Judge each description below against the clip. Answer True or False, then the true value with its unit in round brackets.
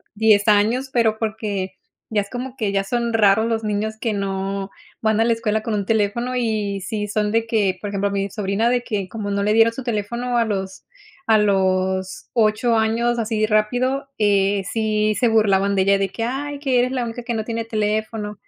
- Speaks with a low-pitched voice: False (215 Hz)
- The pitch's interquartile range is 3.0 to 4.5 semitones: False (2.4 semitones)